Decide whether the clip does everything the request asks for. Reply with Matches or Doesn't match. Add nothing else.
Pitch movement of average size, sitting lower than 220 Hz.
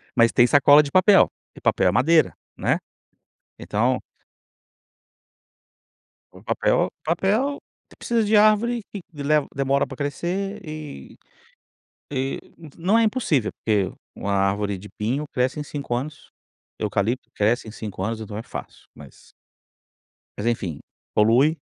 Doesn't match